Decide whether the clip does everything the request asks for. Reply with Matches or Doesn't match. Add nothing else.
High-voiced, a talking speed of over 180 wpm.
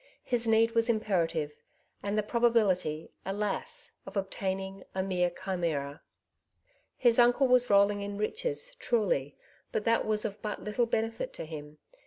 Doesn't match